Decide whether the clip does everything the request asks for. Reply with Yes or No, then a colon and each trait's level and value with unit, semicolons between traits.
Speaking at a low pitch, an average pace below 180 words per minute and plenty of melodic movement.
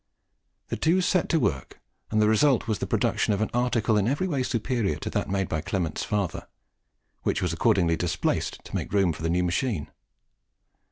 No: low, 105 Hz; average, 190 wpm; wide, 6.0 semitones